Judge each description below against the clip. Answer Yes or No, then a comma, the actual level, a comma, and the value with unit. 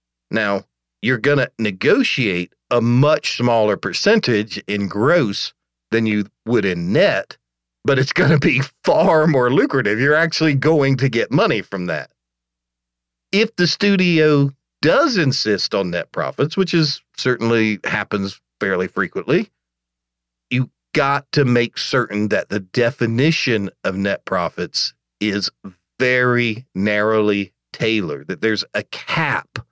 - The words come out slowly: Yes, slow, 130 wpm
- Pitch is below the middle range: Yes, low, 115 Hz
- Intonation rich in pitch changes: Yes, wide, 6.2 semitones